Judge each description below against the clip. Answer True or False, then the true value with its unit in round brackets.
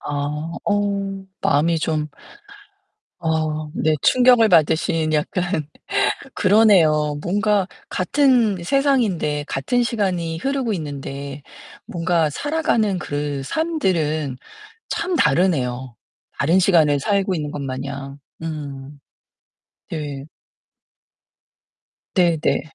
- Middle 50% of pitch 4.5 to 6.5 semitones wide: True (5.5 semitones)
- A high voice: False (165 Hz)